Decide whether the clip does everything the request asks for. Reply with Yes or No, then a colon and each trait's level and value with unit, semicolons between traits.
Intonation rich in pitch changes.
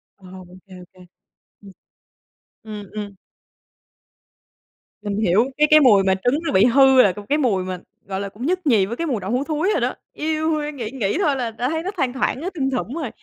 Yes: wide, 6.9 semitones